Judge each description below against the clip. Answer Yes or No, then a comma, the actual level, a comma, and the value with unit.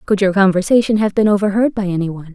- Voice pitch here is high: Yes, high, 200 Hz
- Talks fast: Yes, fast, 230 wpm